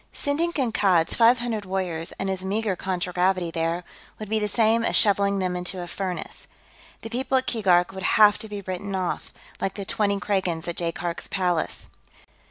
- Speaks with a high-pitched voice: Yes, high, 195 Hz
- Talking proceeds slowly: No, average, 180 wpm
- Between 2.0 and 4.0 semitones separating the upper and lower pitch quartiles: Yes, average, 3.2 semitones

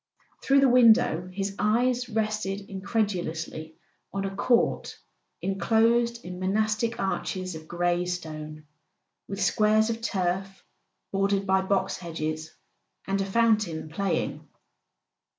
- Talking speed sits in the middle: No, slow, 115 wpm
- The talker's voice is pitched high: Yes, high, 195 Hz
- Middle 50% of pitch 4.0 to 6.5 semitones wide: No, average, 3.5 semitones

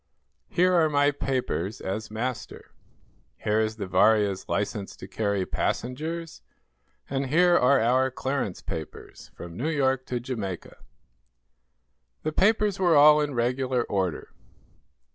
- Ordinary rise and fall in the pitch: No, wide, 5.8 semitones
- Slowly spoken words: Yes, slow, 125 wpm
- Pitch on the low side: Yes, low, 125 Hz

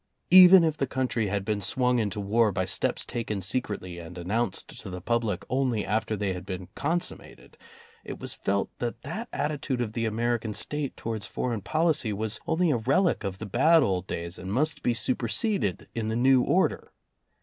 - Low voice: Yes, low, 115 Hz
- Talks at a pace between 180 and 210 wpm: Yes, average, 185 wpm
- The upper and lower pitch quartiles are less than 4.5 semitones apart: No, average, 4.8 semitones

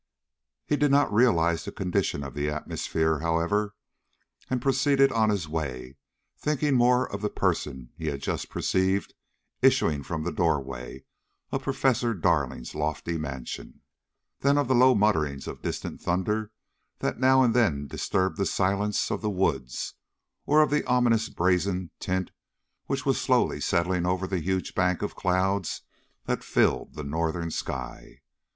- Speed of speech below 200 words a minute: Yes, average, 155 wpm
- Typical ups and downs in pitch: No, wide, 6.4 semitones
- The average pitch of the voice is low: Yes, very low, 95 Hz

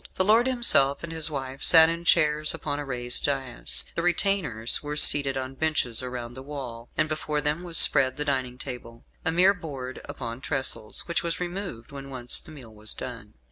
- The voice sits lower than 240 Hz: Yes, medium, 140 Hz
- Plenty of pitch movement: No, average, 4.3 semitones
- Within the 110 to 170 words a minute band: No, average, 195 wpm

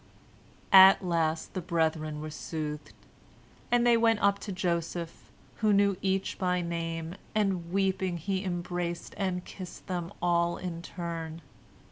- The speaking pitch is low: No, medium, 175 Hz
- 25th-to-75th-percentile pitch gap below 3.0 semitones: Yes, narrow, 2.4 semitones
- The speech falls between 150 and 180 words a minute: No, slow, 135 wpm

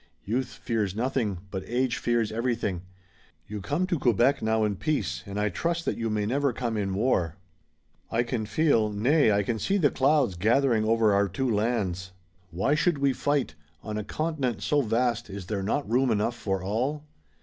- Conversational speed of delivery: Yes, average, 185 wpm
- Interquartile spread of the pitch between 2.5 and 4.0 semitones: No, average, 4.5 semitones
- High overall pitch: No, low, 115 Hz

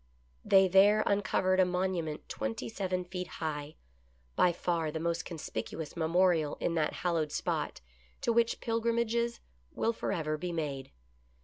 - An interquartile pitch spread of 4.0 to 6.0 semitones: No, average, 3.4 semitones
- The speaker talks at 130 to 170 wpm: Yes, slow, 135 wpm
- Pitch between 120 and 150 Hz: No, medium, 175 Hz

